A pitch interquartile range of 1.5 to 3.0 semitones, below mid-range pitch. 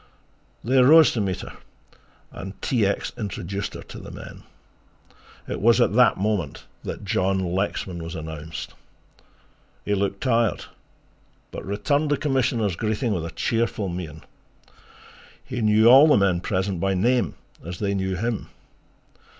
No: average, 4.2 semitones; low, 100 Hz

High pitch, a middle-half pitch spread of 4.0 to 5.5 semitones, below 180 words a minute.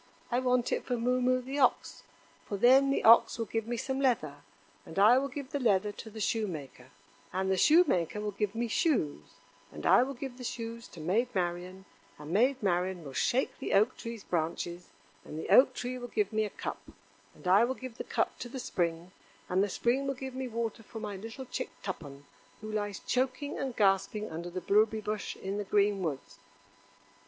No: high, 215 Hz; average, 5.0 semitones; fast, 205 wpm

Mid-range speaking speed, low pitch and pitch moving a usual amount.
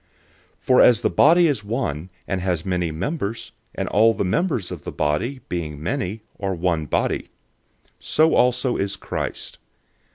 No: average, 160 wpm; low, 100 Hz; wide, 6.2 semitones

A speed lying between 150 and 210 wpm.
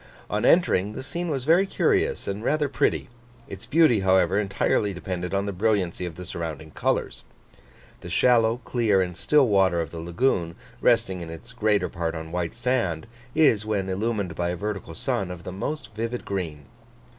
Yes: average, 180 wpm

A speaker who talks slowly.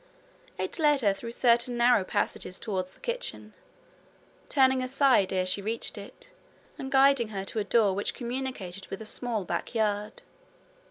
No: average, 160 wpm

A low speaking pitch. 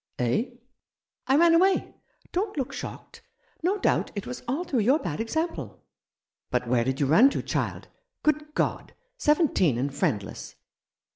No: very high, 250 Hz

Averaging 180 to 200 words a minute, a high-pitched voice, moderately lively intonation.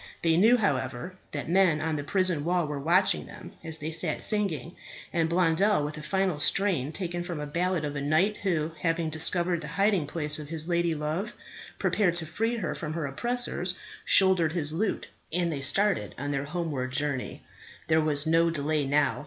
No: average, 185 wpm; medium, 165 Hz; average, 3.4 semitones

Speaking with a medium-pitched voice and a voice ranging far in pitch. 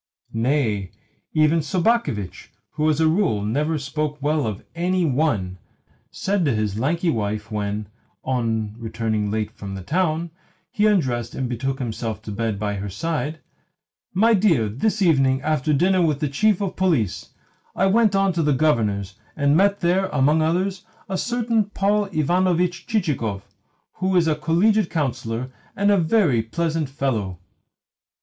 Yes: medium, 150 Hz; wide, 8.2 semitones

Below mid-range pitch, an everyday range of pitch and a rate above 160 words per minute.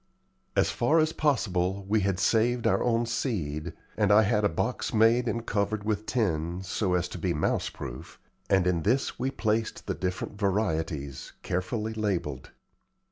Yes: low, 100 Hz; average, 4.0 semitones; average, 170 wpm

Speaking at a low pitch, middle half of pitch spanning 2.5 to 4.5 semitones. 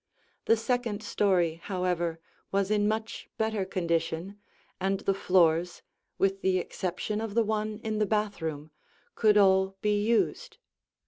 No: high, 195 Hz; average, 2.8 semitones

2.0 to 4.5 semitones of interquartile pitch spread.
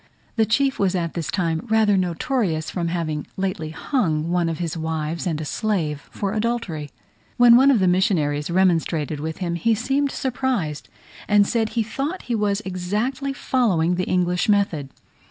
No: wide, 5.6 semitones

